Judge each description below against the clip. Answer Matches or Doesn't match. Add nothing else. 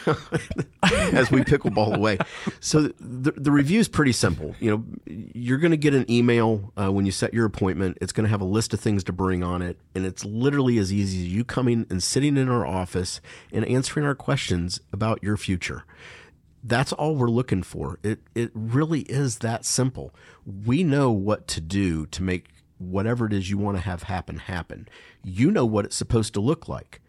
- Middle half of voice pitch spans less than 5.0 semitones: Doesn't match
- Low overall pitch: Matches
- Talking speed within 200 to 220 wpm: Matches